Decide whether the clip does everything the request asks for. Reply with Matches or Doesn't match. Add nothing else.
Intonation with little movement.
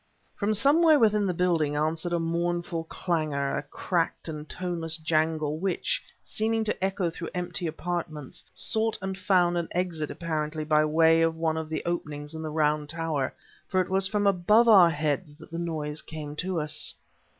Doesn't match